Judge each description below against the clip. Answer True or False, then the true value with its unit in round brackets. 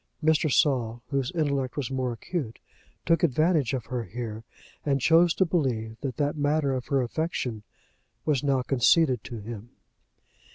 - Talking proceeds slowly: False (155 wpm)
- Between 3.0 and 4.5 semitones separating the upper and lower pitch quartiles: True (4.2 semitones)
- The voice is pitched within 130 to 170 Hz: True (135 Hz)